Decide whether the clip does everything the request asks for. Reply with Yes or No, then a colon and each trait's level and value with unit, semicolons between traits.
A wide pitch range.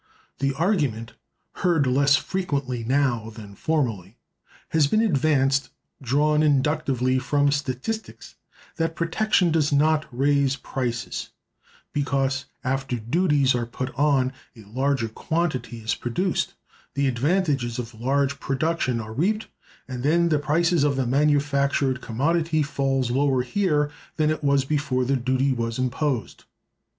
No: average, 3.1 semitones